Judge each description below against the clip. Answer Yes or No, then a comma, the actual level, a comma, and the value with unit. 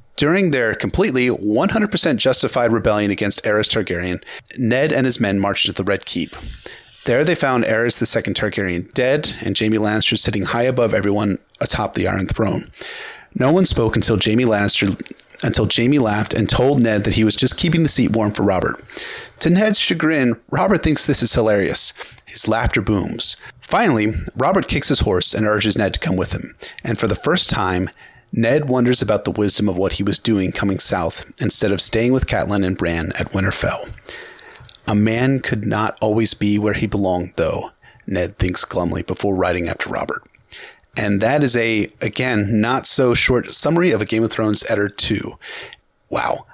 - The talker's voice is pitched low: Yes, low, 110 Hz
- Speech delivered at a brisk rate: No, average, 180 wpm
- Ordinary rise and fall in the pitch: Yes, average, 3.6 semitones